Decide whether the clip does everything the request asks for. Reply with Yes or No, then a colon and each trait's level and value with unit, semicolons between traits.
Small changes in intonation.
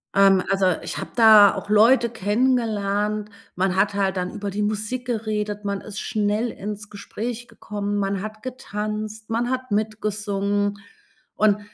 Yes: narrow, 1.4 semitones